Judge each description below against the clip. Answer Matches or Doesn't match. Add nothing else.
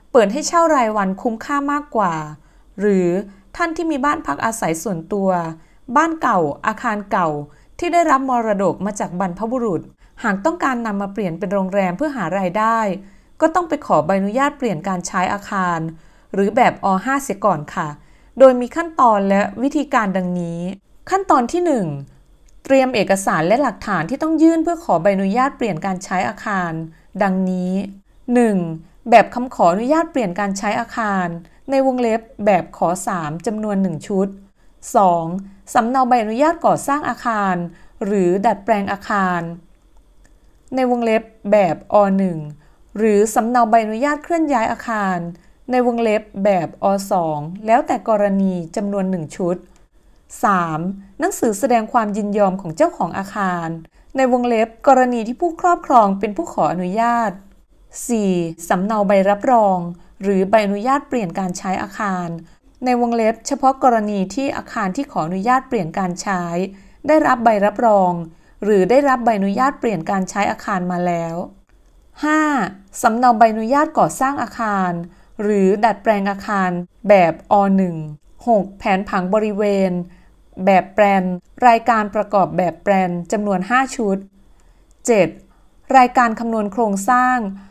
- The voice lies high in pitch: Matches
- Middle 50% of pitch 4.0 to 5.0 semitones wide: Matches